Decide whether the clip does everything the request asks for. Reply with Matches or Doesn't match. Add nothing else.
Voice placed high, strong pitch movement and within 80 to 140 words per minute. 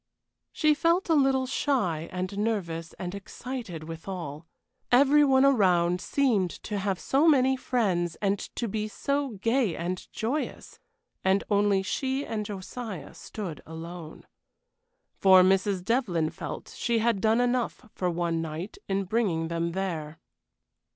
Matches